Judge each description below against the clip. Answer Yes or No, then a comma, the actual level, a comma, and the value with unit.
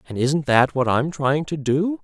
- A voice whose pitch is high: No, medium, 145 Hz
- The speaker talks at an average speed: No, fast, 235 wpm